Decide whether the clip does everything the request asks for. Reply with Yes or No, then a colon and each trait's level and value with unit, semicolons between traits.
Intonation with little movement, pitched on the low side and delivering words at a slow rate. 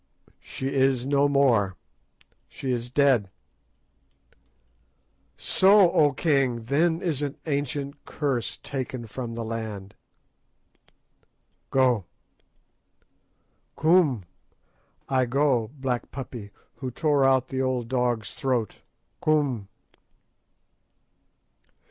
No: average, 3.0 semitones; low, 130 Hz; slow, 90 wpm